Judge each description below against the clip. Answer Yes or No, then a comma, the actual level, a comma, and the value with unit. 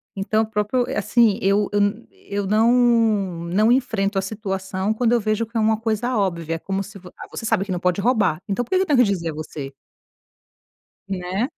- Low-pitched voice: No, high, 205 Hz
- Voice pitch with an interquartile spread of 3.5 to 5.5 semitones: No, average, 2.9 semitones